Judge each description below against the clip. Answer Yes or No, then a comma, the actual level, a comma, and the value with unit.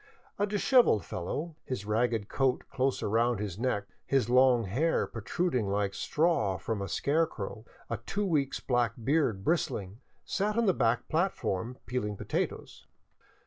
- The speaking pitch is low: Yes, low, 125 Hz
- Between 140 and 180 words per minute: Yes, average, 150 wpm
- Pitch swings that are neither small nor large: No, wide, 6.9 semitones